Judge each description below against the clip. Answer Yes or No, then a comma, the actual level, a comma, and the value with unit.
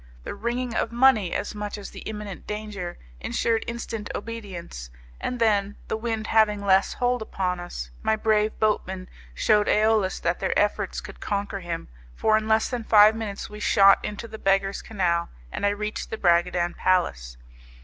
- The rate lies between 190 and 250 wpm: No, average, 170 wpm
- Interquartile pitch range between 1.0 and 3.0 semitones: Yes, narrow, 2.5 semitones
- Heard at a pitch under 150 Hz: No, high, 210 Hz